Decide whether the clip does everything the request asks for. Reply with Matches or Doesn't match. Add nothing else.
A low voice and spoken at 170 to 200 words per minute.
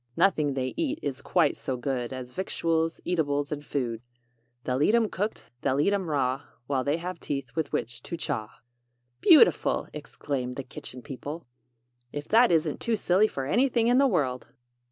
Doesn't match